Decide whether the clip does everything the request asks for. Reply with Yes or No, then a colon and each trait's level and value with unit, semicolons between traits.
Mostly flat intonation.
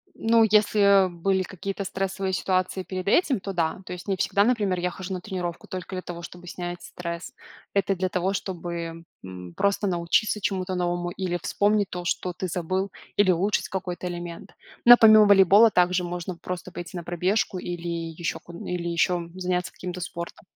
Yes: narrow, 1.9 semitones